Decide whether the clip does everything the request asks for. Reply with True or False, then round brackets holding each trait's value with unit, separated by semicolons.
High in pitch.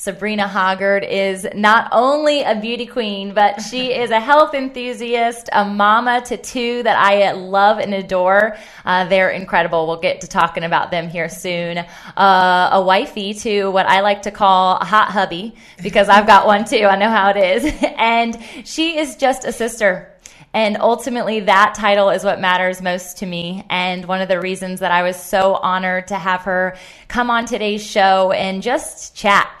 True (200 Hz)